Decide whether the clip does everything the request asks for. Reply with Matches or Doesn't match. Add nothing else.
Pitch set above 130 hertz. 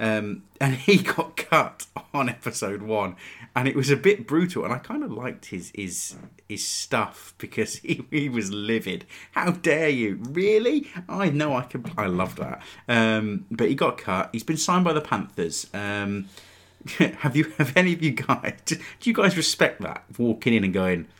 Matches